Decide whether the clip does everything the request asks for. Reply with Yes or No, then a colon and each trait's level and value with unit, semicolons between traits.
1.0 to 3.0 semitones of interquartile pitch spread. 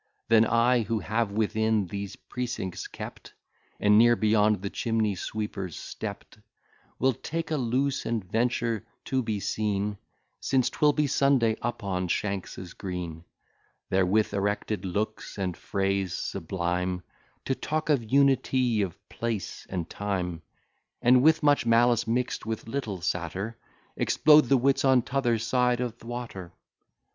No: average, 4.0 semitones